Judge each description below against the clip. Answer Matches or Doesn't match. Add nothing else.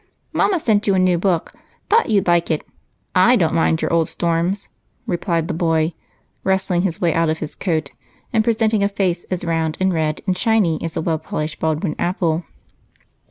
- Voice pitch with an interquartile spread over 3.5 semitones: Doesn't match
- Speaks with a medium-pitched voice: Matches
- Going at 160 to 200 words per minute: Matches